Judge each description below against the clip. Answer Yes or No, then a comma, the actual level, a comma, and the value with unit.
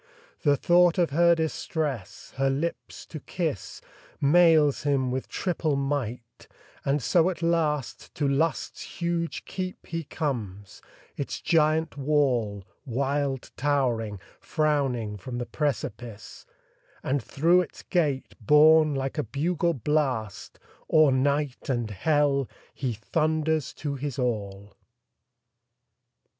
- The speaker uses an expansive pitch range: No, average, 4.0 semitones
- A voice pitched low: No, medium, 145 Hz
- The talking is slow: Yes, slow, 115 wpm